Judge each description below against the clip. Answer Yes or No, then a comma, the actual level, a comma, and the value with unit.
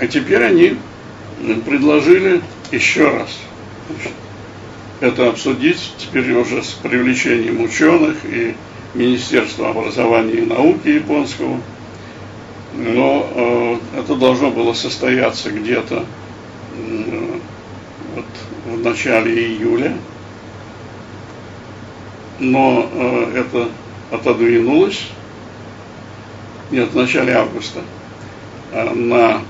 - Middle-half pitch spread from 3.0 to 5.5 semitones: Yes, average, 4.4 semitones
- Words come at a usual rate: No, slow, 85 wpm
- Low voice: Yes, low, 115 Hz